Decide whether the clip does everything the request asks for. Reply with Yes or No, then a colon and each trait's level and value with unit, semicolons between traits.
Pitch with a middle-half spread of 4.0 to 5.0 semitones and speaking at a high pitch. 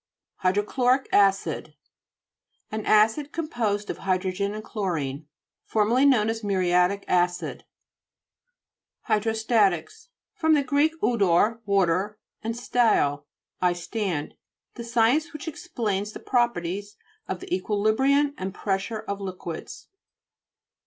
Yes: average, 4.3 semitones; high, 210 Hz